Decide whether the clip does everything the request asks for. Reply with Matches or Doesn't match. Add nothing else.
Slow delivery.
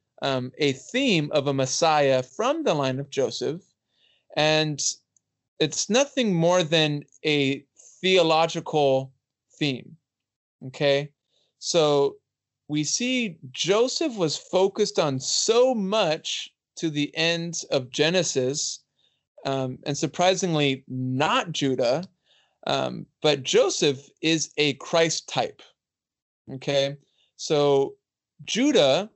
Matches